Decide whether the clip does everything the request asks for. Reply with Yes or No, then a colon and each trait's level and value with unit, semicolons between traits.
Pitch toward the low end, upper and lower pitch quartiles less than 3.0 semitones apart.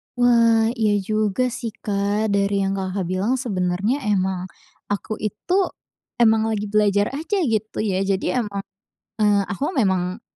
No: high, 210 Hz; narrow, 2.6 semitones